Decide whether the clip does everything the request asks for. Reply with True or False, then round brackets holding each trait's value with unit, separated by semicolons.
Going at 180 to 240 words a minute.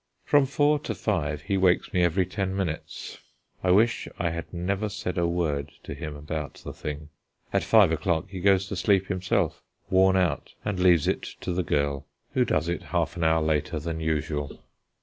True (190 wpm)